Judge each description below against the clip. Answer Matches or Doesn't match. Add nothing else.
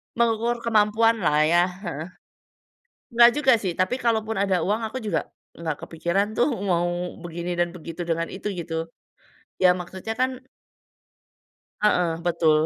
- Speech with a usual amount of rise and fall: Matches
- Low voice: Doesn't match